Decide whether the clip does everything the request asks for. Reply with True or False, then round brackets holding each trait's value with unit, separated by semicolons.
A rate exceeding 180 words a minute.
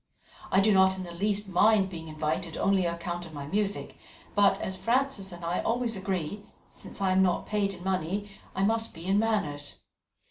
True (200 wpm)